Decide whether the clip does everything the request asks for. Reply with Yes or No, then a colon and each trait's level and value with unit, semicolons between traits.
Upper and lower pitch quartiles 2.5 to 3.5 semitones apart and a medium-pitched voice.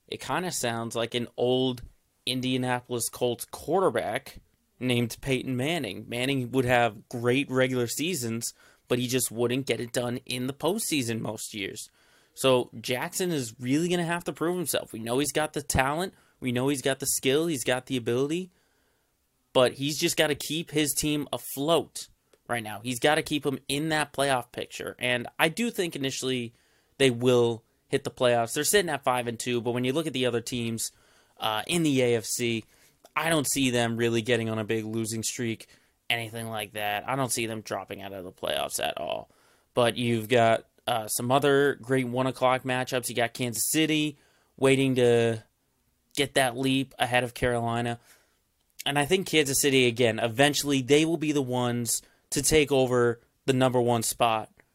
No: average, 3.2 semitones; low, 125 Hz